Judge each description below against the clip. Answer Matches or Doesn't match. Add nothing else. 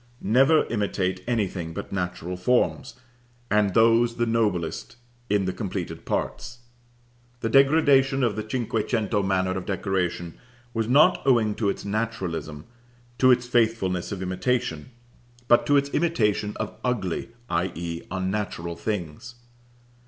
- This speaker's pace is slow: Matches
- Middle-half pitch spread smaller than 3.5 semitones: Doesn't match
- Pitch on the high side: Doesn't match